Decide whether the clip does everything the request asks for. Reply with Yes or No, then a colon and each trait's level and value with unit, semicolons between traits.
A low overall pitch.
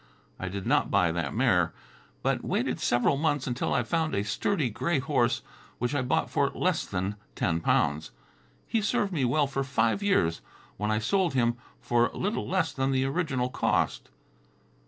Yes: low, 130 Hz